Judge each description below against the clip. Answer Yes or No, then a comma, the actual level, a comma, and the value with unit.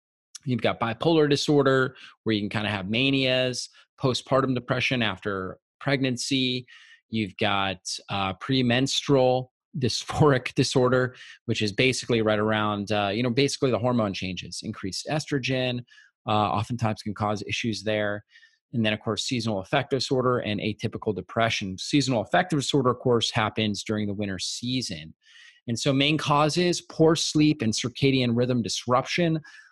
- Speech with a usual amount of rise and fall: Yes, average, 4.0 semitones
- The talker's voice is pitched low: Yes, low, 120 Hz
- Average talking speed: Yes, average, 145 wpm